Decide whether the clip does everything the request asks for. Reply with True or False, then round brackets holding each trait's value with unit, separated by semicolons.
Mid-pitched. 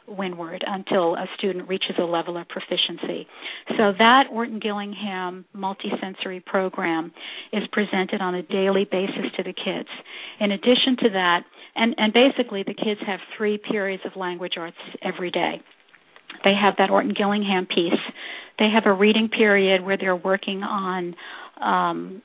False (195 Hz)